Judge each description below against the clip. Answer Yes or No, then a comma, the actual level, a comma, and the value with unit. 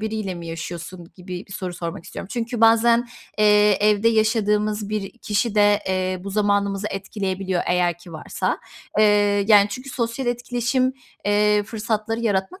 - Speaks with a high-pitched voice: Yes, high, 210 Hz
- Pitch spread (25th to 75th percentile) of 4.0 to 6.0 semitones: No, average, 2.8 semitones